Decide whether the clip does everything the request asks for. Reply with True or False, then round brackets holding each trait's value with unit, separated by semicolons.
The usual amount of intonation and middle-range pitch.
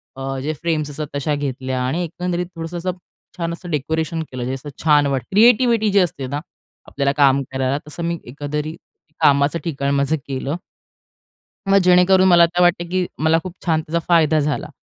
True (3.7 semitones; 155 Hz)